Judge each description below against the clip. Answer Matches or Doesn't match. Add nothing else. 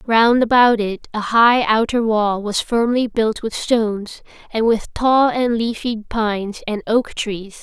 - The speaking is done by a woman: Matches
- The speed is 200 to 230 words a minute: Doesn't match